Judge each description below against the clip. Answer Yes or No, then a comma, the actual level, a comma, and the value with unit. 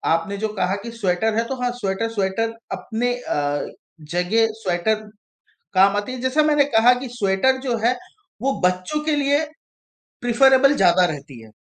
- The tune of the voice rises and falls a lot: Yes, wide, 5.7 semitones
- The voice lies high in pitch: Yes, high, 225 Hz